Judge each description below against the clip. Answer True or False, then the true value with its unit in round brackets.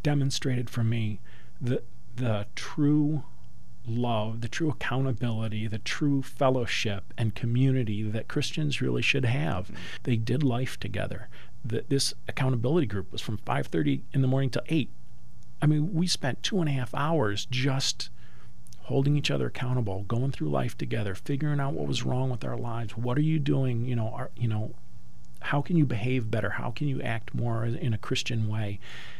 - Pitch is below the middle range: True (120 Hz)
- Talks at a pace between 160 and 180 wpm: True (175 wpm)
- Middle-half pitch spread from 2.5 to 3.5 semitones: False (4.3 semitones)